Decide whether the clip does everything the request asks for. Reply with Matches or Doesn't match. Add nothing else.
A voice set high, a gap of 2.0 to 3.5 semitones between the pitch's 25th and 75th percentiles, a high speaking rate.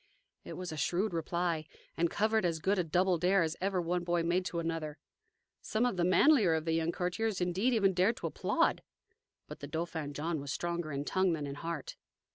Doesn't match